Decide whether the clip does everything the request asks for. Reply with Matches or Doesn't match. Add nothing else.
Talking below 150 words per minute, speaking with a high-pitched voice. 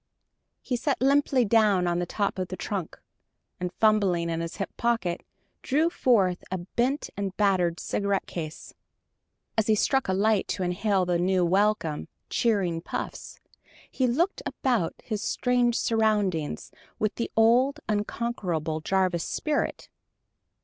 Matches